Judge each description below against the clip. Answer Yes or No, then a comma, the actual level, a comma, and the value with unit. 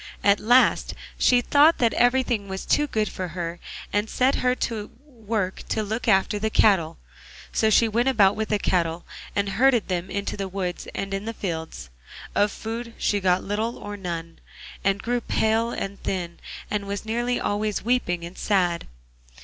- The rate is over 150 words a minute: Yes, average, 175 wpm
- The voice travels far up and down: No, average, 3.4 semitones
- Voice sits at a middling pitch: No, high, 205 Hz